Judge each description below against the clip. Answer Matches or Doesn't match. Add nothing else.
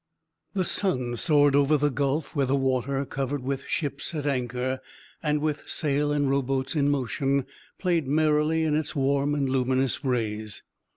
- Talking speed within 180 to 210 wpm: Doesn't match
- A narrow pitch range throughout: Matches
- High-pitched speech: Doesn't match